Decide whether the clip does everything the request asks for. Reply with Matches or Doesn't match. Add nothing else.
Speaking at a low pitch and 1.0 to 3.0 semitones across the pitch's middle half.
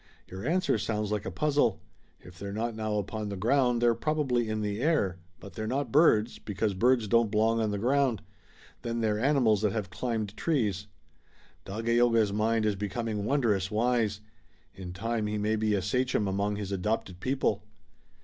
Matches